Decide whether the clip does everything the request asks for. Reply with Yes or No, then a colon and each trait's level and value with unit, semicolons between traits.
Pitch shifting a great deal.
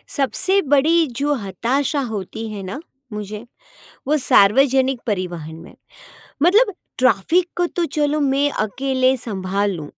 Yes: wide, 6.2 semitones